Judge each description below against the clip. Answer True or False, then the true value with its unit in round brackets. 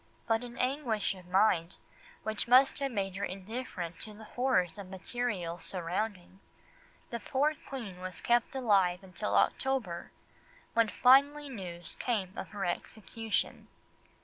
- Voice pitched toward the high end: True (210 Hz)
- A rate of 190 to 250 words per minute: False (140 wpm)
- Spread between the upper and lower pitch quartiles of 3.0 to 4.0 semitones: False (5.0 semitones)